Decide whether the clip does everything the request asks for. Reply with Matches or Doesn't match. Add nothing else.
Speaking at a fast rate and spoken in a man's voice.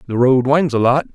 Matches